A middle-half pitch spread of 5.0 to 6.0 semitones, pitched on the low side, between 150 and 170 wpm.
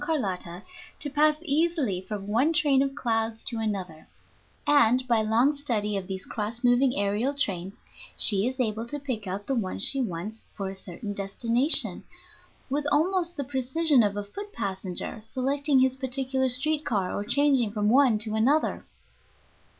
No: wide, 5.4 semitones; high, 240 Hz; average, 165 wpm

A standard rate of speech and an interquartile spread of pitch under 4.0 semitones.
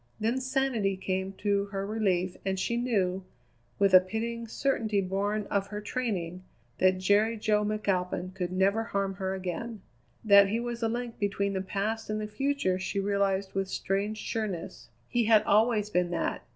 Yes: average, 170 wpm; average, 2.7 semitones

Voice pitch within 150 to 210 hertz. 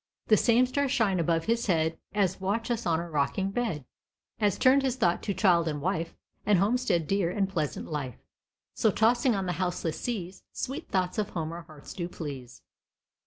Yes: high, 190 Hz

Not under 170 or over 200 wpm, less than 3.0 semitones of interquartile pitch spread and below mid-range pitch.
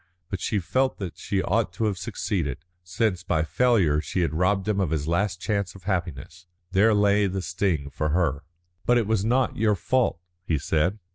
No: average, 195 wpm; average, 4.0 semitones; very low, 95 Hz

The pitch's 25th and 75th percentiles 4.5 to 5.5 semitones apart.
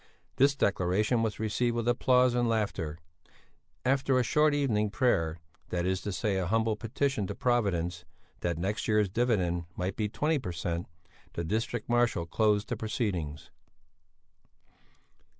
Yes: average, 5.0 semitones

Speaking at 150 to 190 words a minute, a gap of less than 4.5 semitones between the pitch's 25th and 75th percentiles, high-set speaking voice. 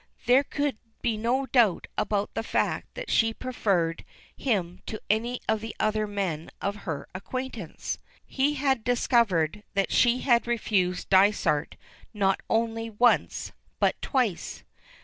No: slow, 135 wpm; average, 3.9 semitones; high, 220 Hz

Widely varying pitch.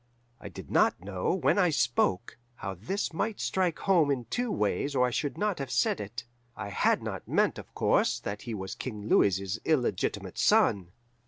Yes: wide, 8.1 semitones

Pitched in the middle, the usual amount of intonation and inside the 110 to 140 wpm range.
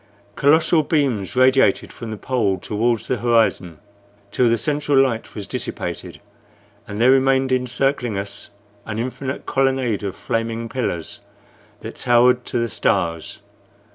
No: low, 120 Hz; average, 3.2 semitones; slow, 135 wpm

